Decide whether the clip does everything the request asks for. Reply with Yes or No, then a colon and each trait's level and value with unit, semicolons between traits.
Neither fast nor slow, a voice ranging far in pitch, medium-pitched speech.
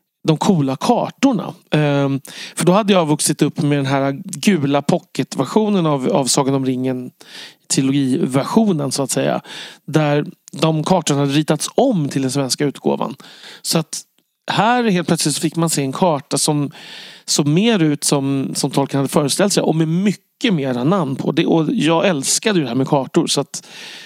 No: average, 175 wpm; average, 4.6 semitones; medium, 155 Hz